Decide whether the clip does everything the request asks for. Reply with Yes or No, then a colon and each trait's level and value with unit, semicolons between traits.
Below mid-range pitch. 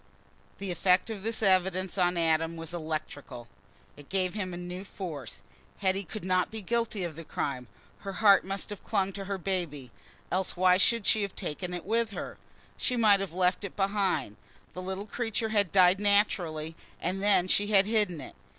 No: high, 190 Hz